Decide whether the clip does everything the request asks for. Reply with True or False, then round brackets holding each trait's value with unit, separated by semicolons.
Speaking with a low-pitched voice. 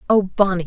False (190 Hz)